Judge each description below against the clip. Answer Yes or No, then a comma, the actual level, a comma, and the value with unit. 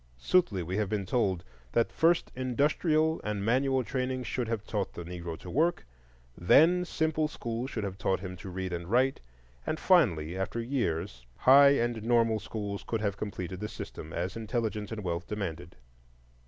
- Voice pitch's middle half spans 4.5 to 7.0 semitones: Yes, wide, 5.6 semitones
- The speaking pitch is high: No, low, 110 Hz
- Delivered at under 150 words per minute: No, average, 170 wpm